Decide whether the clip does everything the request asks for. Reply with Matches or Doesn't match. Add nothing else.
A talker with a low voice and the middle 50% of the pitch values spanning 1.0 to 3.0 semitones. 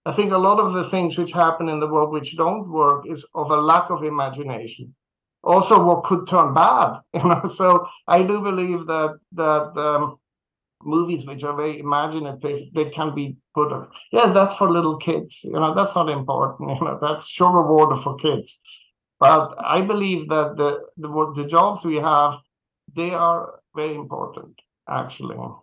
Doesn't match